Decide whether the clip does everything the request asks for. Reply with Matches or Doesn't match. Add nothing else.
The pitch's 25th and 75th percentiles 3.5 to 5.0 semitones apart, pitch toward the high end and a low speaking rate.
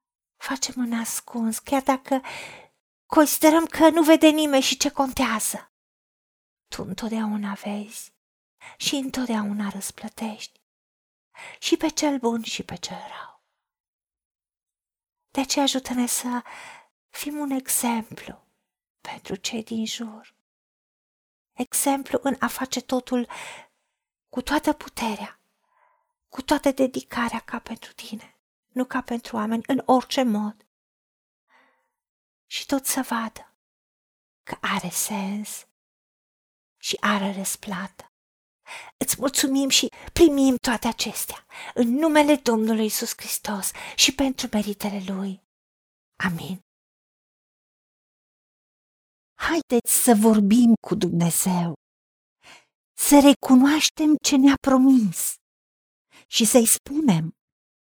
Matches